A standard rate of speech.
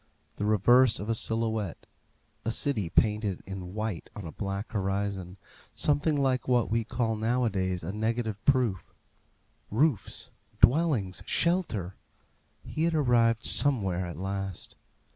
No: slow, 125 wpm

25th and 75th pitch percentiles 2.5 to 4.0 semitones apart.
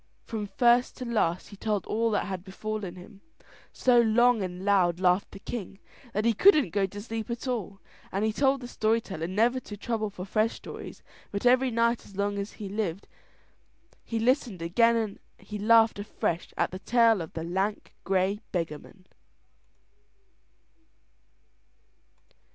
Yes: average, 3.3 semitones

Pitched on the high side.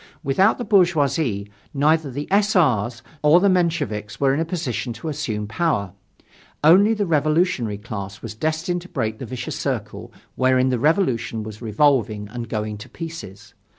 No: low, 135 Hz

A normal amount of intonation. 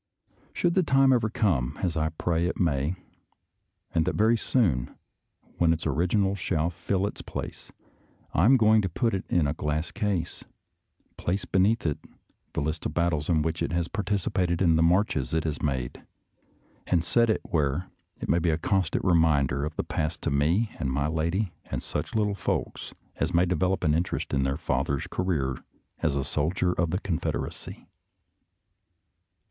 Yes: average, 3.9 semitones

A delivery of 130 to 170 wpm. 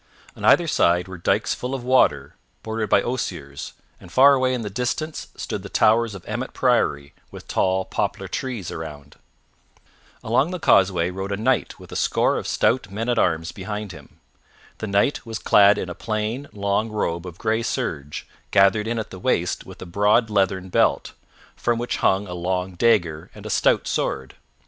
No: average, 185 wpm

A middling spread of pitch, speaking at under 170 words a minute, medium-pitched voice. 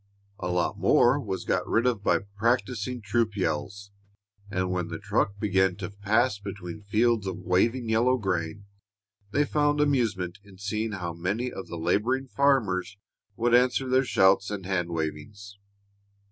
No: average, 4.4 semitones; average, 155 wpm; low, 100 Hz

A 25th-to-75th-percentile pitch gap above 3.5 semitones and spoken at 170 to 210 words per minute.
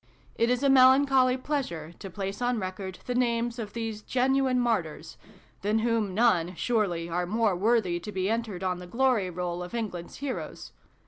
Yes: average, 5.2 semitones; average, 185 wpm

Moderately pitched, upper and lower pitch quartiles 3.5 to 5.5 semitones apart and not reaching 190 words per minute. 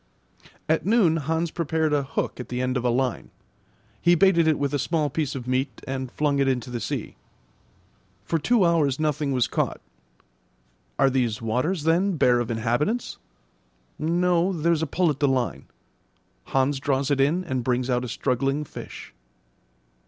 Yes: medium, 145 Hz; average, 4.2 semitones; average, 170 wpm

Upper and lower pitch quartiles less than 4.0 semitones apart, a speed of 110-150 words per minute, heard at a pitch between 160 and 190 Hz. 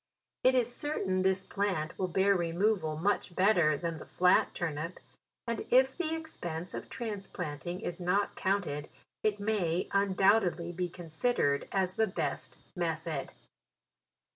Yes: average, 3.5 semitones; average, 140 wpm; medium, 185 Hz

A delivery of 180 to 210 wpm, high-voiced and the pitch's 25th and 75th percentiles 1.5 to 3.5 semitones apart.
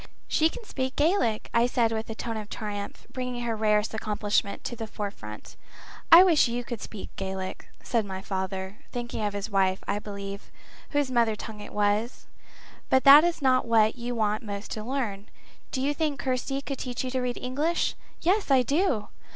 No: average, 190 wpm; high, 230 Hz; average, 4.0 semitones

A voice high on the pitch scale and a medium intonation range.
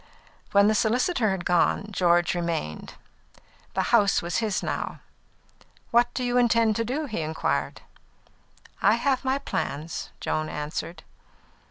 No: high, 210 Hz; wide, 6.0 semitones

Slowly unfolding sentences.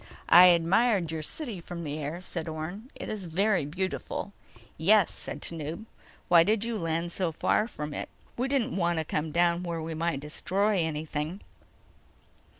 No: average, 165 wpm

